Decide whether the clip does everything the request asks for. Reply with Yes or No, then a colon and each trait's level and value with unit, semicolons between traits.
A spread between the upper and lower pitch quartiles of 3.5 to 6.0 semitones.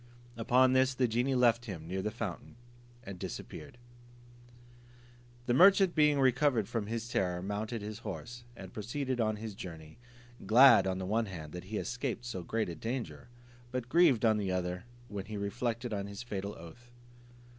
Yes: average, 3.9 semitones